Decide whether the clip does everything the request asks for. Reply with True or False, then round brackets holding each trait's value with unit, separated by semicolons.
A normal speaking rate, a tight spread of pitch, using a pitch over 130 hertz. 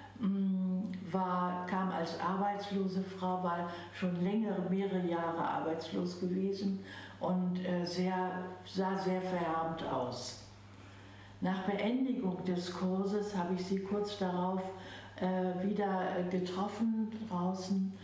False (100 wpm; 1.5 semitones; 185 Hz)